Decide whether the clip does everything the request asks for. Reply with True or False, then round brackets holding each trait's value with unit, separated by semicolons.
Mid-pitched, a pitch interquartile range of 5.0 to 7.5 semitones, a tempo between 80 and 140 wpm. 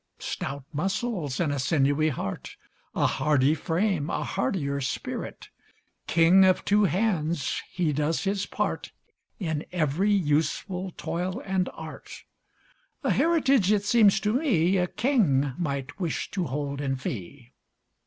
True (170 Hz; 5.4 semitones; 135 wpm)